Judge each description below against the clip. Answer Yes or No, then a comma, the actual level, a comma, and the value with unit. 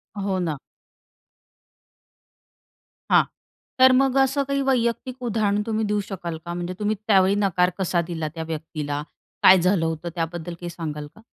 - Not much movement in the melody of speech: No, average, 4.6 semitones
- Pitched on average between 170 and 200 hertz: Yes, medium, 185 Hz